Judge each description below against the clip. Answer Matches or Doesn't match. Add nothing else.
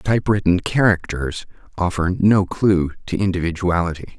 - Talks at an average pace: Doesn't match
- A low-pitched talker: Matches